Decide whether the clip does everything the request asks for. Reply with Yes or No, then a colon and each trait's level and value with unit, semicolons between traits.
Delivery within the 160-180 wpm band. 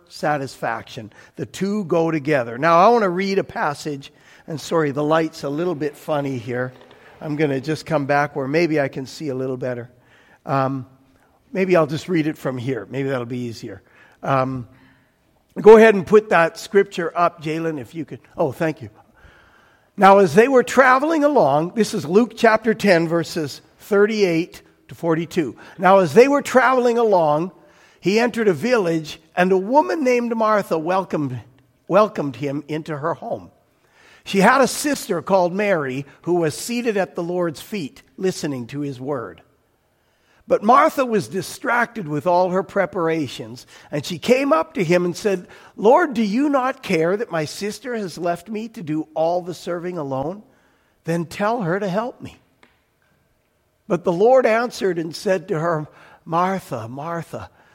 Yes: average, 170 wpm